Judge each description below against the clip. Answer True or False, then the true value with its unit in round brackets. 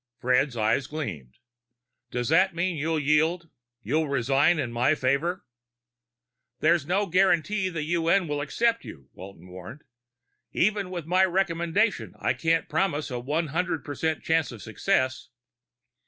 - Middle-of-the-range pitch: True (160 Hz)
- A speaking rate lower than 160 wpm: True (140 wpm)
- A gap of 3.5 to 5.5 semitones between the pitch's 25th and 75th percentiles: True (4.7 semitones)